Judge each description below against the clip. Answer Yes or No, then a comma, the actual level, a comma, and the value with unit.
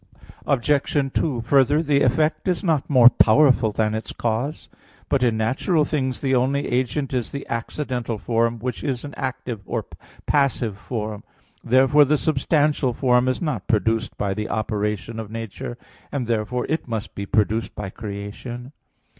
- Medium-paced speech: Yes, average, 160 wpm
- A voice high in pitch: No, low, 125 Hz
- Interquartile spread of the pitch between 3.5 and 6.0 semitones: Yes, average, 4.1 semitones